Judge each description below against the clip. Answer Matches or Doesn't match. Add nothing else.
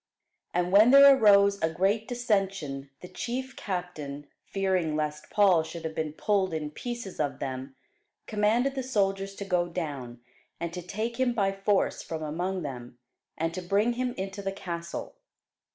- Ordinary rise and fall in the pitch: Matches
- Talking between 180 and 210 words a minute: Doesn't match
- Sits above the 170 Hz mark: Matches